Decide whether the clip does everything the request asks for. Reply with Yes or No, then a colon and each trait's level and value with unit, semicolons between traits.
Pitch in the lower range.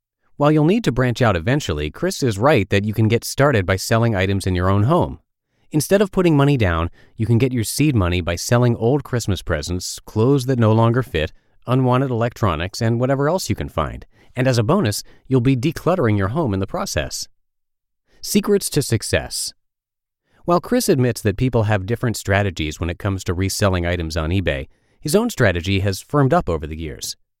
Yes: low, 115 Hz